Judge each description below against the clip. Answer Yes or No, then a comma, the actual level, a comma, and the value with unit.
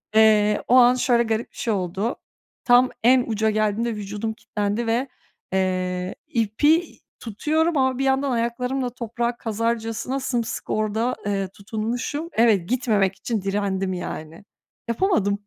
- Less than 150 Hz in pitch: No, high, 225 Hz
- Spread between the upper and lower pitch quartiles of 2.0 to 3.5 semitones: Yes, average, 3.2 semitones